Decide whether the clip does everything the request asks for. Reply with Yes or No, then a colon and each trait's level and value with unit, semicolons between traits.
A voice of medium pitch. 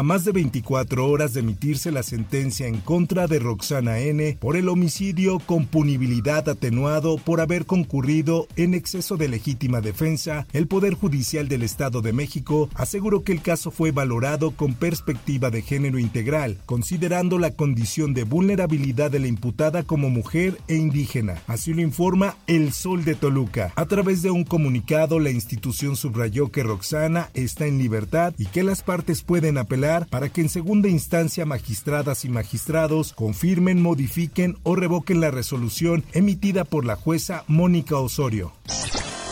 Yes: medium, 155 Hz